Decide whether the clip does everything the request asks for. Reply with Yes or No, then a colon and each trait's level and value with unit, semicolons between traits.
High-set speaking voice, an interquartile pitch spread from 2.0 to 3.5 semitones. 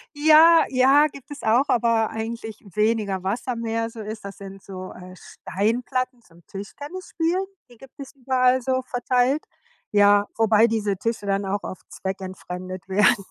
No: high, 225 Hz; average, 4.4 semitones